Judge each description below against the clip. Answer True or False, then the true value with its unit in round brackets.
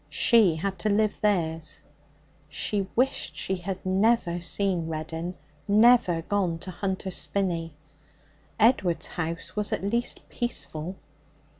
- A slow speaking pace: True (120 wpm)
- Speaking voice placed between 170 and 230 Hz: True (190 Hz)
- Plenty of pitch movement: False (3.8 semitones)